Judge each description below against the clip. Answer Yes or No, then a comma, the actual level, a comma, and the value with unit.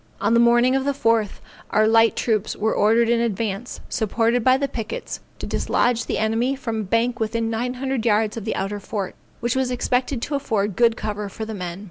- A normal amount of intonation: No, narrow, 2.3 semitones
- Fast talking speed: Yes, fast, 210 wpm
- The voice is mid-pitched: No, high, 230 Hz